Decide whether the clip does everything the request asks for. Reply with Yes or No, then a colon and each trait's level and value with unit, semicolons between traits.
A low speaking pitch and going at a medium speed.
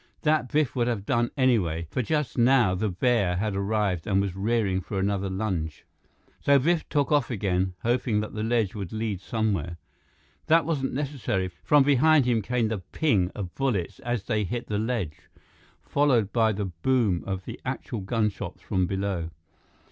Yes: low, 110 Hz; average, 170 wpm